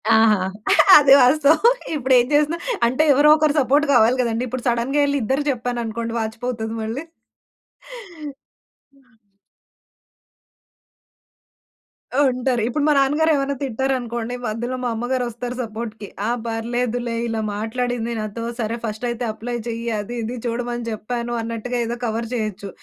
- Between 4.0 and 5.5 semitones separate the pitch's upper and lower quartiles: No, narrow, 2.4 semitones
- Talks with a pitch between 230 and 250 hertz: Yes, high, 240 Hz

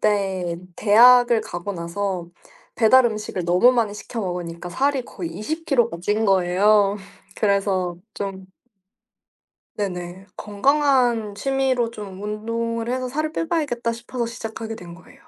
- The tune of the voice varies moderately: Yes, average, 4.2 semitones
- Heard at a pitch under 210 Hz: No, high, 215 Hz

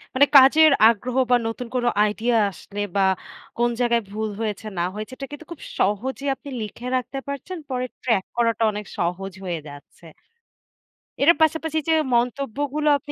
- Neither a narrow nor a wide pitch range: Yes, average, 4.8 semitones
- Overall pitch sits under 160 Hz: No, high, 240 Hz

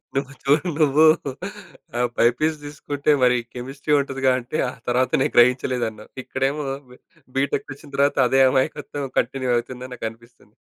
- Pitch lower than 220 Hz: Yes, low, 135 Hz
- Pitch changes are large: No, narrow, 2.4 semitones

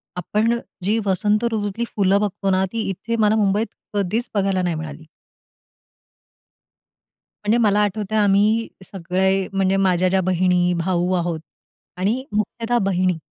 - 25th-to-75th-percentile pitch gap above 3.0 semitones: No, narrow, 2.4 semitones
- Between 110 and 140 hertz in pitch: No, high, 195 Hz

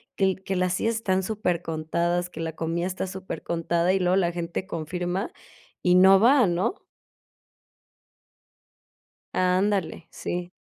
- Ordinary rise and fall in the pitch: No, narrow, 1.9 semitones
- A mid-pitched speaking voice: Yes, medium, 180 Hz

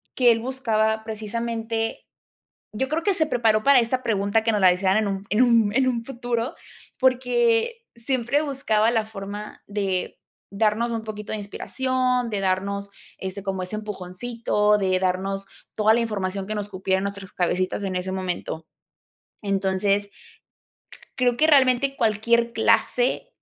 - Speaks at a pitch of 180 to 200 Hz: No, high, 220 Hz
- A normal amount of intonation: Yes, average, 3.5 semitones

